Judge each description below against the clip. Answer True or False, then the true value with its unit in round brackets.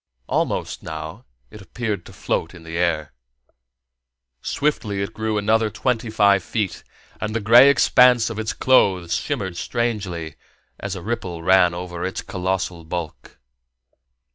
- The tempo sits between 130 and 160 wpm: True (140 wpm)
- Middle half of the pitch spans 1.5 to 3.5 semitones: False (4.0 semitones)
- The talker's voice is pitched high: False (100 Hz)